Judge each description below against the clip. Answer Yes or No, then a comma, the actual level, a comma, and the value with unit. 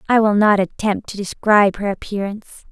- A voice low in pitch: No, high, 205 Hz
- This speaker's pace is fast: No, average, 175 wpm